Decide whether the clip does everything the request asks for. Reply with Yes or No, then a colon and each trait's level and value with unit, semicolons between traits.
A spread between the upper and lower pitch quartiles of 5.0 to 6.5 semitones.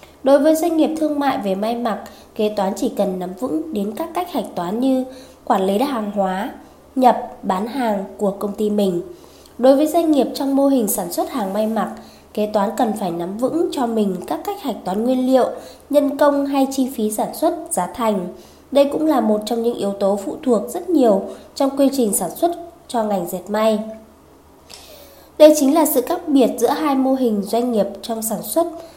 Yes: wide, 5.4 semitones